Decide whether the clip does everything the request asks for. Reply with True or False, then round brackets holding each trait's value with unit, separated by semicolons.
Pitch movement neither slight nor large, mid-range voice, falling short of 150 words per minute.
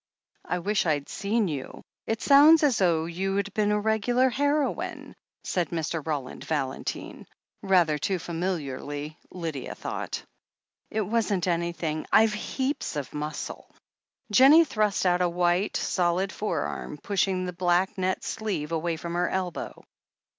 True (4.3 semitones; 180 Hz; 140 wpm)